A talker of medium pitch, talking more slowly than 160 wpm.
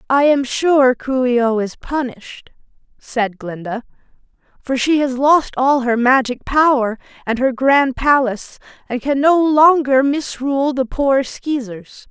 No: very high, 260 Hz; average, 150 wpm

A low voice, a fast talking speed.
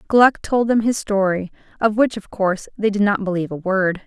No: high, 205 Hz; fast, 220 wpm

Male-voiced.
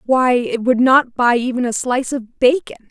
No: female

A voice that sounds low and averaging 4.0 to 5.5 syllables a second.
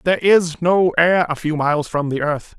No: medium, 165 Hz; 5.0 syllables/s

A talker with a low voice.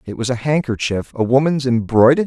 Yes: low, 125 Hz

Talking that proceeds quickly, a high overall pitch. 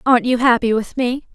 Yes: fast, 225 wpm; high, 245 Hz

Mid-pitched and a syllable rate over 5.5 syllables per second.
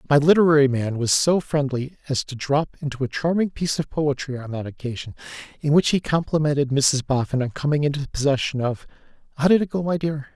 Yes: medium, 145 Hz; 5.9 syllables/s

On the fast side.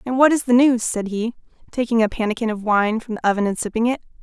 Yes: fast, 255 wpm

